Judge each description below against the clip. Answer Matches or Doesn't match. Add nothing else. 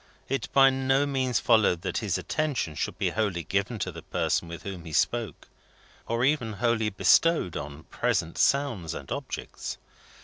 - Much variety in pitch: Matches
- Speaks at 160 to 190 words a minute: Matches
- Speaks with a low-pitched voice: Matches